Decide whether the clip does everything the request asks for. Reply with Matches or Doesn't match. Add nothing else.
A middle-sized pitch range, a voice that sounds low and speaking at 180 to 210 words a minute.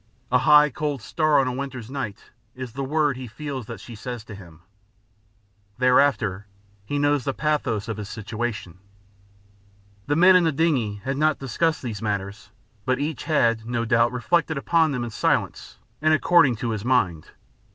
Doesn't match